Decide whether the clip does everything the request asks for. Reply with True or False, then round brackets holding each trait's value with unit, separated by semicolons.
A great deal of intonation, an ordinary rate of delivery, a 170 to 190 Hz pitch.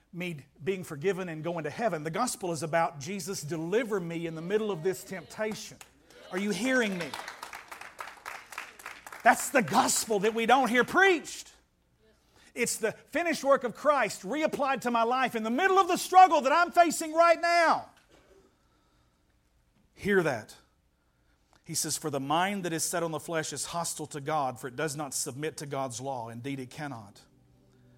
True (7.9 semitones; 175 wpm; 185 Hz)